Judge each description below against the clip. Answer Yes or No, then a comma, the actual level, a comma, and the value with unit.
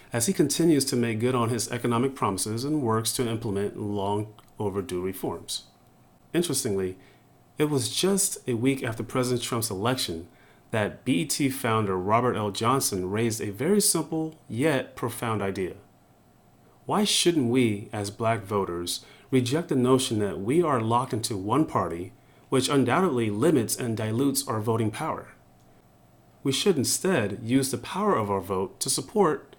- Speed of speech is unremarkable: Yes, average, 150 wpm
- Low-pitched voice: Yes, low, 120 Hz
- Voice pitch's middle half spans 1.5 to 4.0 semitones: No, average, 4.5 semitones